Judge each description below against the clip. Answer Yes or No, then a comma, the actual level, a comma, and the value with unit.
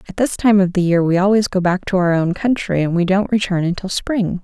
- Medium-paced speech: No, fast, 270 wpm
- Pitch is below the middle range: No, high, 190 Hz